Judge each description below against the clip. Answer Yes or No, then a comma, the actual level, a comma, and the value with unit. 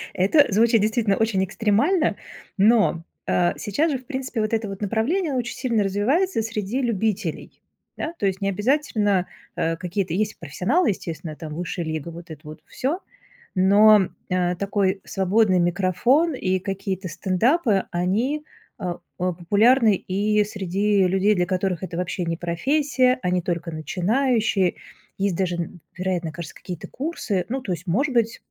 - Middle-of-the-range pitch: No, high, 200 Hz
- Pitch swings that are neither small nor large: Yes, average, 4.3 semitones